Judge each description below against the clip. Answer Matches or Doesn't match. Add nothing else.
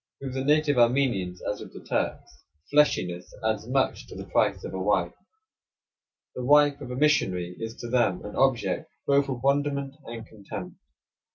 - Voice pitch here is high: Doesn't match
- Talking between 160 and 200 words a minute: Matches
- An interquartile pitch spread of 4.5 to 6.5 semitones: Matches